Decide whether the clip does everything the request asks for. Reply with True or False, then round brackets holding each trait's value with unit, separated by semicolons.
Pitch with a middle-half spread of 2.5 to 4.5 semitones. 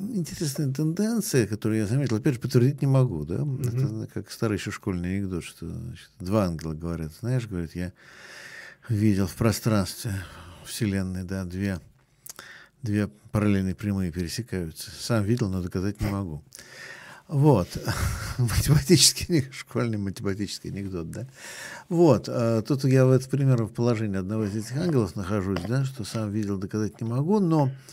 False (5.0 semitones)